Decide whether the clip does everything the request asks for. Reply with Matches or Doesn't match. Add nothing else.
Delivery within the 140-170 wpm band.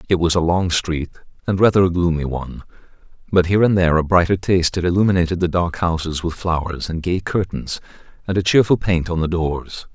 Doesn't match